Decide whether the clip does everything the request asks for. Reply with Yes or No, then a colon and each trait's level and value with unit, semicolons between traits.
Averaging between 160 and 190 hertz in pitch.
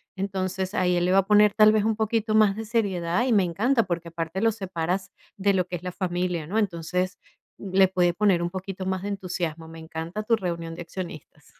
Yes: medium, 185 Hz